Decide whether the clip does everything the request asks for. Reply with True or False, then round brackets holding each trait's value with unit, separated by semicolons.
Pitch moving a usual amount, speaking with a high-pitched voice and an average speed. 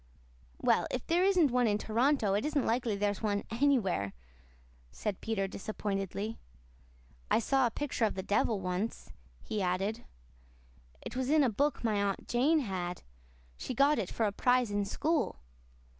True (4.7 semitones; 220 Hz; 160 wpm)